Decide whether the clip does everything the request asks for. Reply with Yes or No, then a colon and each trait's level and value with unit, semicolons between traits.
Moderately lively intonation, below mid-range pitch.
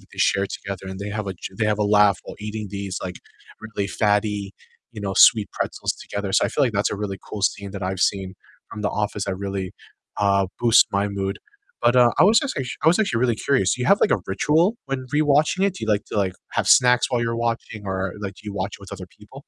Yes: average, 3.2 semitones; low, 105 Hz